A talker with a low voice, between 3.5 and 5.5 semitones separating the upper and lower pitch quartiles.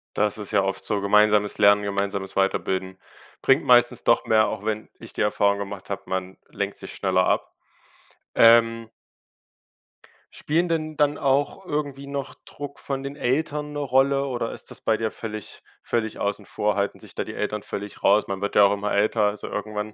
Yes: low, 105 Hz; average, 5.2 semitones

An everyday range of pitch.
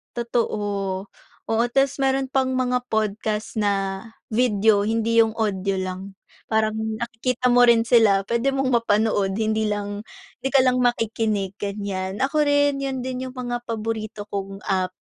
Yes: average, 3.5 semitones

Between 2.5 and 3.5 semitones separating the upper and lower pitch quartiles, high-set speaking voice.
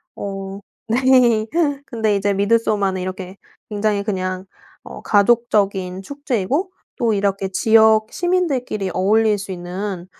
Yes: average, 3.0 semitones; high, 205 Hz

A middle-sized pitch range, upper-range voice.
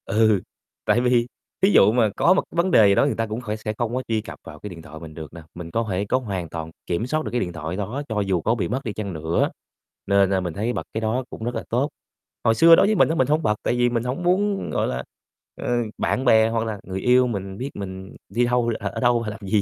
No: average, 4.2 semitones; low, 110 Hz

